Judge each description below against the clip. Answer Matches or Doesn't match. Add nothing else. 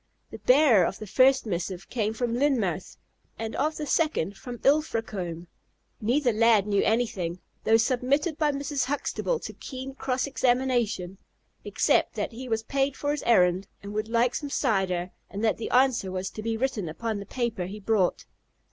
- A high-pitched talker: Matches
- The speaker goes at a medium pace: Matches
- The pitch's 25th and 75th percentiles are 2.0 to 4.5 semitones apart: Doesn't match